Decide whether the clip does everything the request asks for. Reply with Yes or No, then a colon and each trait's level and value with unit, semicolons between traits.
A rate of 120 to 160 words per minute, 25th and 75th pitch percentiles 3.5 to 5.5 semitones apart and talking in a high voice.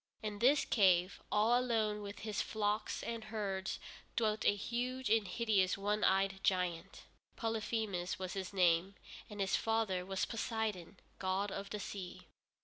No: average, 145 wpm; narrow, 2.6 semitones; high, 205 Hz